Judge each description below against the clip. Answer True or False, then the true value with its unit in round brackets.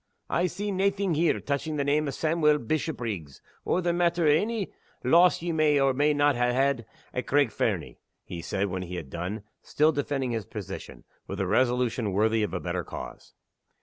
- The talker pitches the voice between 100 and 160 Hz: True (140 Hz)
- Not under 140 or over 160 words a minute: False (190 wpm)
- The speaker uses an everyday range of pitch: False (6.8 semitones)